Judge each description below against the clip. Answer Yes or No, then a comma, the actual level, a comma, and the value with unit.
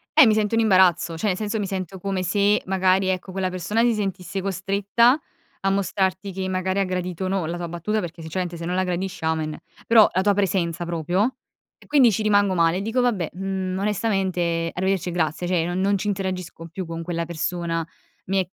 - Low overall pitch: No, medium, 185 Hz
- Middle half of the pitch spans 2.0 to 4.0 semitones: Yes, narrow, 2.4 semitones